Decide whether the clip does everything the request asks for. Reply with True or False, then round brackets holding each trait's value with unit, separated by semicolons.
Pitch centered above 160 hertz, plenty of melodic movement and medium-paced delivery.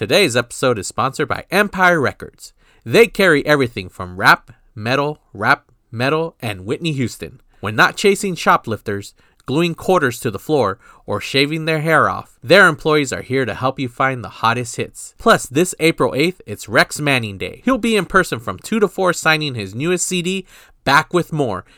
False (140 Hz; 6.4 semitones; 180 wpm)